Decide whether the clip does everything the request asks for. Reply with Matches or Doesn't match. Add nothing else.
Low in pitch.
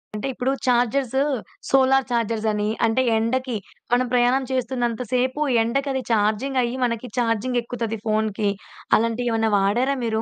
Doesn't match